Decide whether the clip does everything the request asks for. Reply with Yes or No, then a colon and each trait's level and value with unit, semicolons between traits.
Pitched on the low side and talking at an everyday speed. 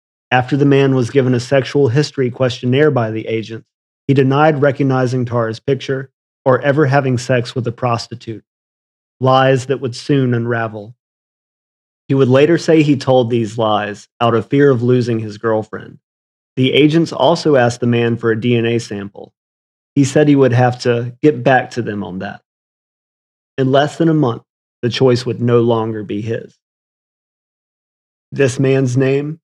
Yes: low, 125 Hz; average, 165 wpm